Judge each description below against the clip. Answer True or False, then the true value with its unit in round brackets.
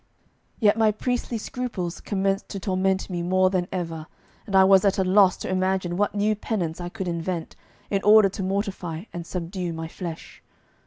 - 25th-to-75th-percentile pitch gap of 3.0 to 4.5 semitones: False (2.4 semitones)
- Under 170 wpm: False (180 wpm)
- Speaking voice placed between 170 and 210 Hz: True (190 Hz)